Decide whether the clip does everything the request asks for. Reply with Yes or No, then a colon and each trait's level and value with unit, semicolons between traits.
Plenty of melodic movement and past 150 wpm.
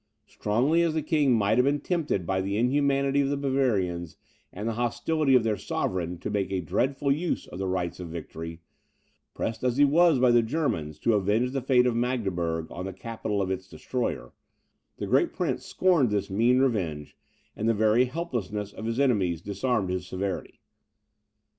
Yes: wide, 6.1 semitones; average, 180 wpm